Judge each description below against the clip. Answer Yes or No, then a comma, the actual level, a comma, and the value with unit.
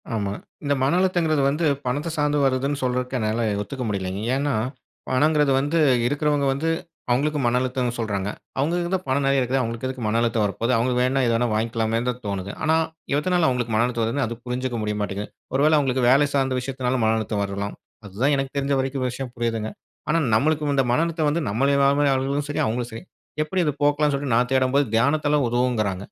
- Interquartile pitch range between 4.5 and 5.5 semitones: No, average, 3.9 semitones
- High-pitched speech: No, low, 130 Hz